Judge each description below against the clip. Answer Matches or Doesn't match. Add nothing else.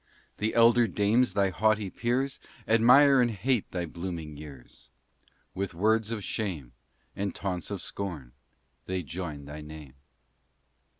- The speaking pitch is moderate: Doesn't match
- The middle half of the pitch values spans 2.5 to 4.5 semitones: Doesn't match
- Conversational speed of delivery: Doesn't match